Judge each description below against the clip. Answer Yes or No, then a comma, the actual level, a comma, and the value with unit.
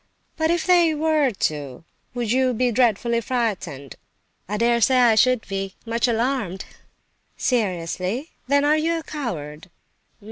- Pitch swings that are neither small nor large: No, wide, 6.0 semitones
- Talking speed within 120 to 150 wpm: Yes, slow, 135 wpm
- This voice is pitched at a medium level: No, high, 235 Hz